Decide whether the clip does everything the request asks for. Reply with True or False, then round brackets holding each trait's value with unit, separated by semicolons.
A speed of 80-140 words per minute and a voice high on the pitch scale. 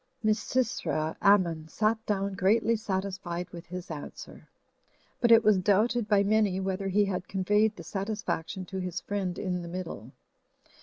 False (150 wpm; 195 Hz)